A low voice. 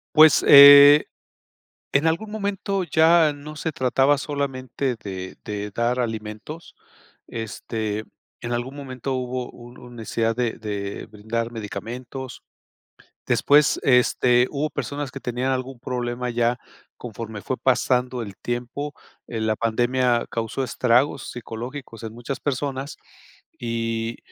Yes: low, 125 Hz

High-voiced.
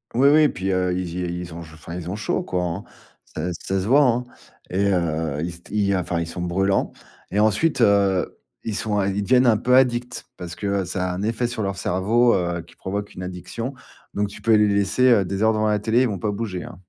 No: low, 100 Hz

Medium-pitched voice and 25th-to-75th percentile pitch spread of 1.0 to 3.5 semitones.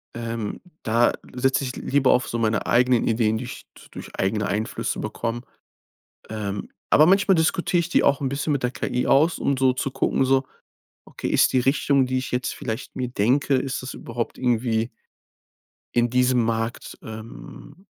No: low, 125 Hz; average, 2.9 semitones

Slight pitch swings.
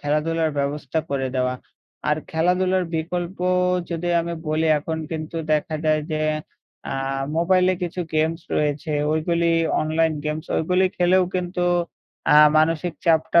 Yes: narrow, 2.3 semitones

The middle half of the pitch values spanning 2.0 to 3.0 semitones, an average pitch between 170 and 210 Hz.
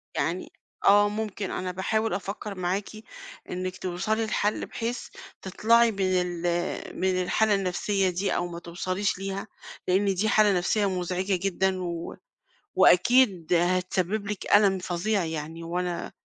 Yes: narrow, 2.4 semitones; high, 190 Hz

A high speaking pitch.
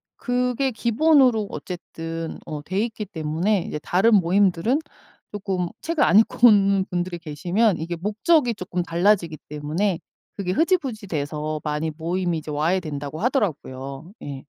No: medium, 180 Hz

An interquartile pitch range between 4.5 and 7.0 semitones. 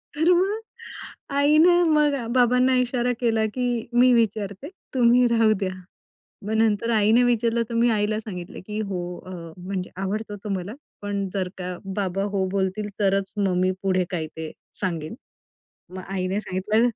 No: average, 4.1 semitones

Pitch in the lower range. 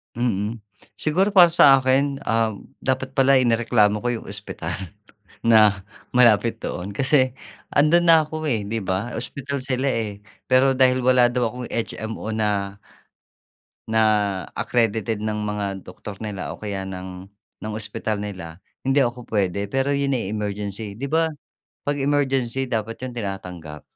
Yes: low, 115 Hz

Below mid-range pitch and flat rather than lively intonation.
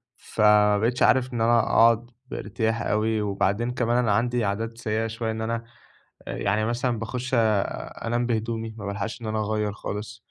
Yes: low, 115 Hz; narrow, 1.7 semitones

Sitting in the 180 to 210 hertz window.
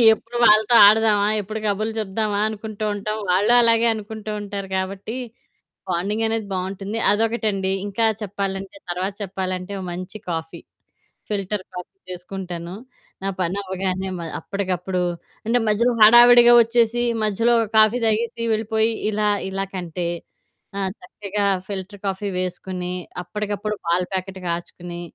Yes: high, 200 Hz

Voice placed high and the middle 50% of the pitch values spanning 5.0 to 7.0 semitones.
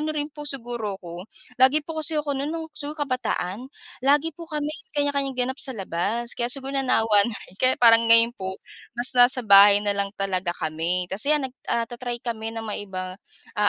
Yes: high, 240 Hz; wide, 5.6 semitones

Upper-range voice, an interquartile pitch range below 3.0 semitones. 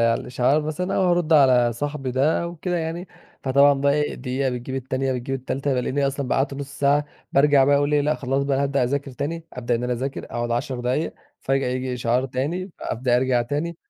No: low, 135 Hz; narrow, 2.6 semitones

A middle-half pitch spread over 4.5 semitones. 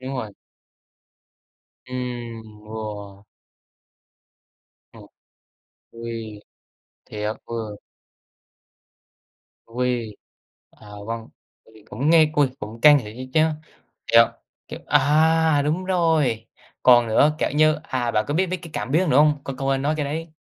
Yes: average, 5.2 semitones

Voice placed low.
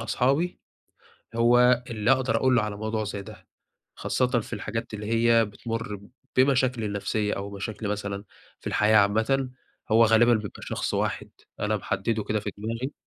Yes: low, 110 Hz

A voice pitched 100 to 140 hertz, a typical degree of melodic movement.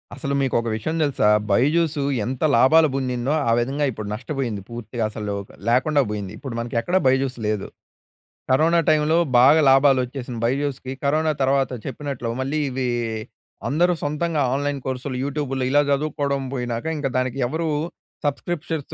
Yes: low, 135 Hz; average, 3.2 semitones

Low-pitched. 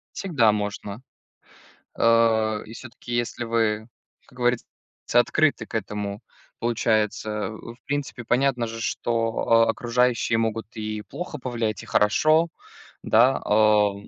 Yes: low, 115 Hz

